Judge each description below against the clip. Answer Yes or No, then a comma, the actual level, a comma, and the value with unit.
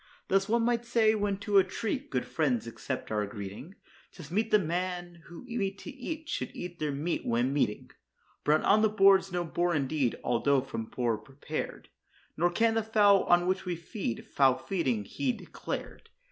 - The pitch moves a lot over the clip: Yes, wide, 7.3 semitones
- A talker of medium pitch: Yes, medium, 175 Hz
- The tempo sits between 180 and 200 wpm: Yes, average, 185 wpm